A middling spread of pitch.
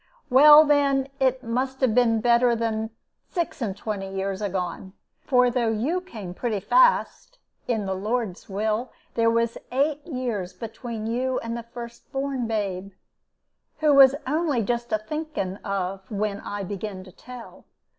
Yes: average, 4.2 semitones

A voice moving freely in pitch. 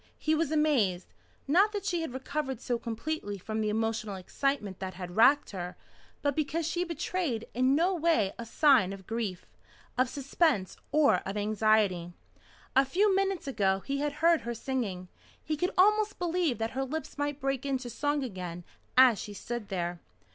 Yes: wide, 6.8 semitones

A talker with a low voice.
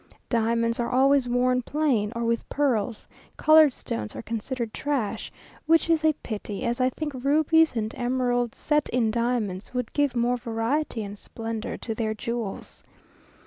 No: high, 240 Hz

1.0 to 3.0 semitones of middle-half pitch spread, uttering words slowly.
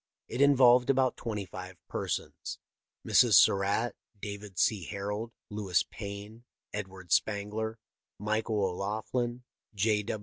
Yes: narrow, 2.5 semitones; slow, 105 wpm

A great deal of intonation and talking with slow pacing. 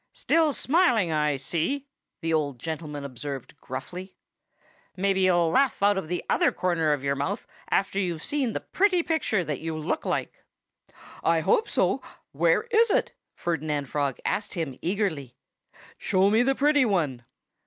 No: wide, 6.9 semitones; average, 155 wpm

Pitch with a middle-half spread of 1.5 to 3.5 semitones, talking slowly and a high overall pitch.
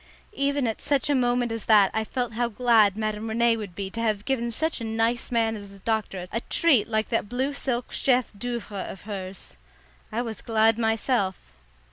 No: narrow, 2.5 semitones; average, 200 wpm; high, 225 Hz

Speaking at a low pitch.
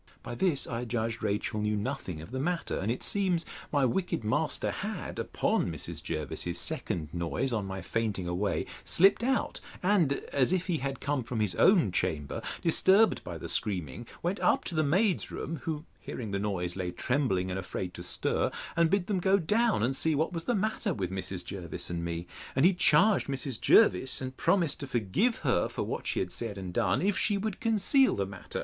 Yes: low, 125 Hz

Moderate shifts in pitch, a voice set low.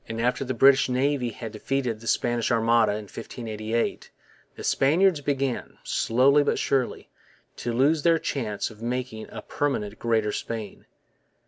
Yes: average, 3.4 semitones; low, 120 Hz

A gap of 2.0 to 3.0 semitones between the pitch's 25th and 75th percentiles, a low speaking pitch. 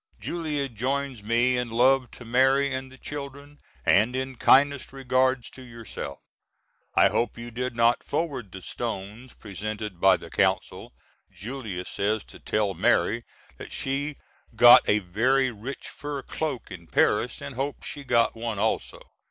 No: average, 3.8 semitones; low, 125 Hz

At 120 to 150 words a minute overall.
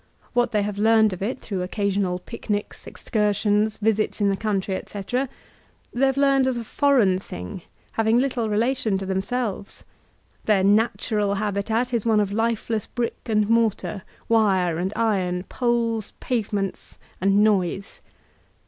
Yes: average, 140 wpm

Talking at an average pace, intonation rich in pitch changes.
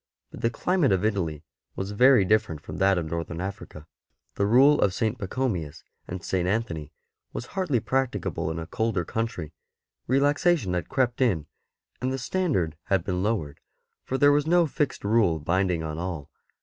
Yes: average, 170 wpm; wide, 7.1 semitones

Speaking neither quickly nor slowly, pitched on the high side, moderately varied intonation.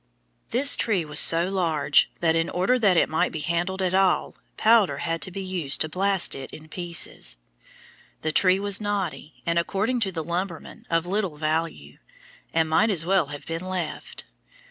No: average, 180 wpm; medium, 175 Hz; average, 3.1 semitones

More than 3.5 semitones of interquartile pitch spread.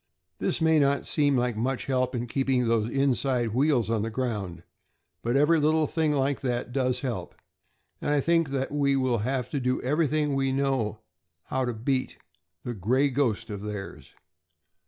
No: average, 3.0 semitones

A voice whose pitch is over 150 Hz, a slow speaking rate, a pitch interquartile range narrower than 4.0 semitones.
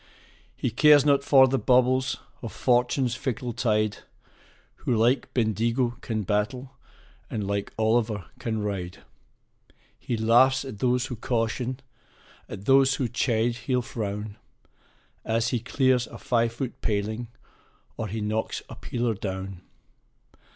No: low, 120 Hz; slow, 130 wpm; average, 3.0 semitones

